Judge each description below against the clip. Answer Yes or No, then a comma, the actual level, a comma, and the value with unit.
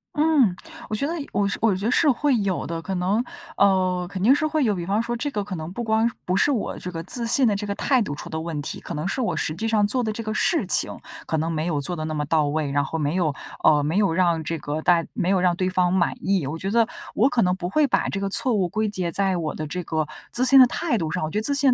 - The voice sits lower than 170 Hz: No, high, 190 Hz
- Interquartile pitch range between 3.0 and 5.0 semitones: No, wide, 5.6 semitones